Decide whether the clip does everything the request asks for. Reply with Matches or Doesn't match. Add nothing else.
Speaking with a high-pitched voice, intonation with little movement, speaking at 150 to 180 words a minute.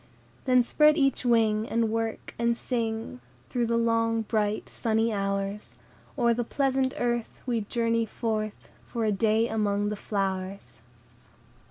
Doesn't match